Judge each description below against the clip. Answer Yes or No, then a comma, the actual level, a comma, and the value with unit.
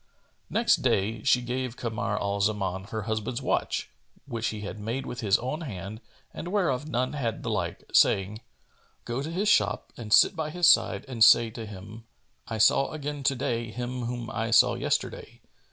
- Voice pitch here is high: No, low, 115 Hz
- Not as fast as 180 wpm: No, average, 185 wpm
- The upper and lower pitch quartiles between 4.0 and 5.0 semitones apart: No, average, 3.5 semitones